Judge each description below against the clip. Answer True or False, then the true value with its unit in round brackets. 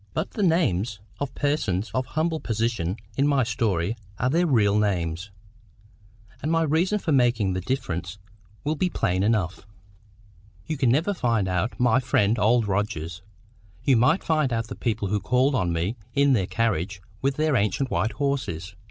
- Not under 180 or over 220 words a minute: False (170 wpm)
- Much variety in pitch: True (6.2 semitones)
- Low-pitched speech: True (115 Hz)